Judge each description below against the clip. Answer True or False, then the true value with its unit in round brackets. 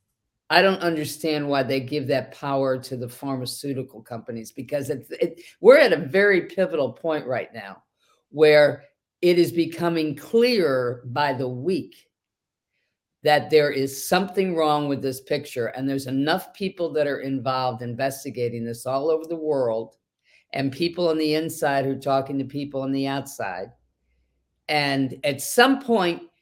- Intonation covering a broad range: False (3.3 semitones)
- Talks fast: False (155 wpm)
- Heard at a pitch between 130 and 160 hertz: True (140 Hz)